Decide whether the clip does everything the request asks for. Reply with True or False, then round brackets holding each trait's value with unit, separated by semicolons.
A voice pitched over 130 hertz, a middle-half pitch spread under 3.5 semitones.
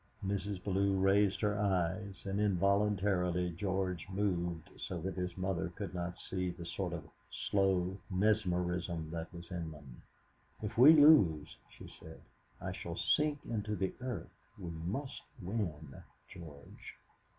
False (95 Hz; 2.8 semitones)